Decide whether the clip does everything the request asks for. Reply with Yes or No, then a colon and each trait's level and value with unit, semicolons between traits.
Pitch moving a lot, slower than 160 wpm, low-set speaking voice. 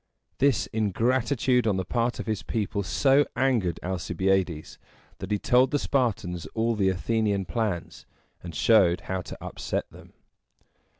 No: average, 4.3 semitones; average, 140 wpm; low, 105 Hz